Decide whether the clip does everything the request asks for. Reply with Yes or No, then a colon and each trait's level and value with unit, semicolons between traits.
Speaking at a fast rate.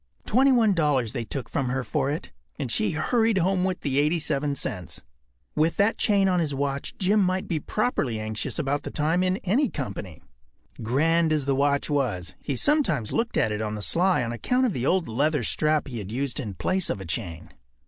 Yes: fast, 210 wpm